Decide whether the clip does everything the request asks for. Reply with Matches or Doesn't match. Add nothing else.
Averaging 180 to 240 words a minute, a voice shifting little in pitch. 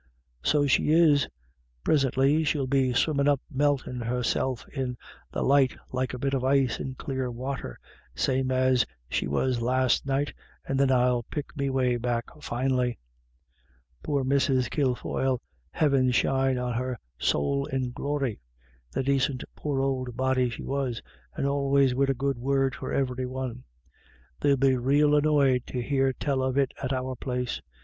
Doesn't match